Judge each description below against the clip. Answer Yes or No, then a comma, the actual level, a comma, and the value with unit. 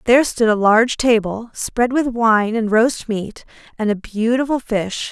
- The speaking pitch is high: Yes, high, 225 Hz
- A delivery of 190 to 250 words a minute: No, average, 175 wpm